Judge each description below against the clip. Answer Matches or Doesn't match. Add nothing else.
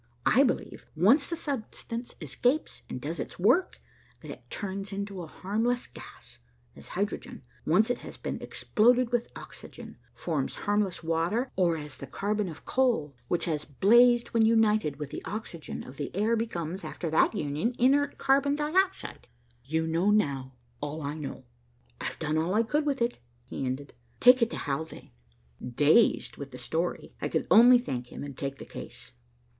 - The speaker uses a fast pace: Doesn't match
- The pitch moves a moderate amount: Doesn't match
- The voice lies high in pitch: Matches